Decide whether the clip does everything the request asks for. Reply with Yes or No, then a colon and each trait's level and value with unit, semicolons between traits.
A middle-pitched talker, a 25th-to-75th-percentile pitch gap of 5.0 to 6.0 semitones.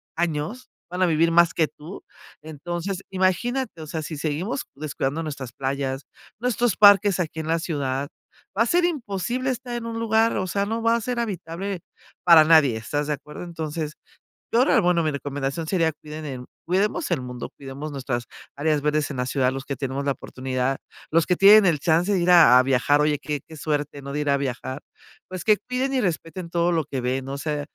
Yes: medium, 160 Hz; average, 5.3 semitones